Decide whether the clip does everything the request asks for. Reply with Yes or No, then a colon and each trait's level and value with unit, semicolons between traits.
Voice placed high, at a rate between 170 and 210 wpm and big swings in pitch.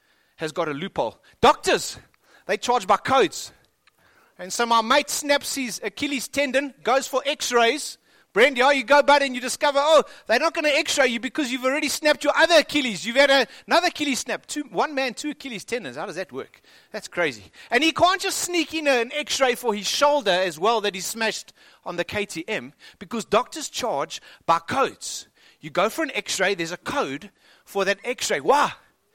Yes: very high, 260 Hz; fast, 205 wpm; wide, 5.8 semitones